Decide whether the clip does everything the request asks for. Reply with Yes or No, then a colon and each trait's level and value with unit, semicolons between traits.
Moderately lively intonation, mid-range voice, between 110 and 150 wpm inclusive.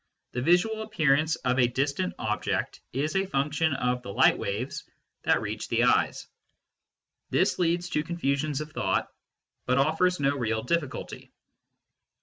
Yes: average, 4.9 semitones; medium, 145 Hz; average, 140 wpm